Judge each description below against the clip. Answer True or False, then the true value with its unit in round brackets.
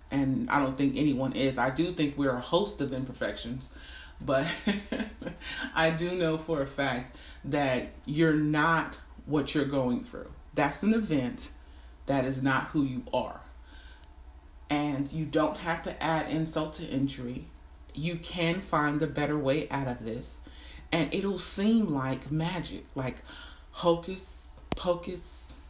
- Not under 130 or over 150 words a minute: True (145 wpm)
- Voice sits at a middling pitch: True (145 Hz)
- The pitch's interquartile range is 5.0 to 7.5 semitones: False (4.3 semitones)